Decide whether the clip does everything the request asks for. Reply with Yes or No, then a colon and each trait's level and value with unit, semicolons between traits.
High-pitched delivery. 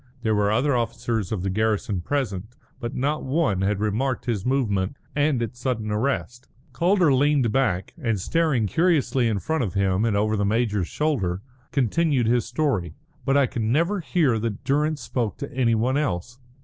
No: low, 120 Hz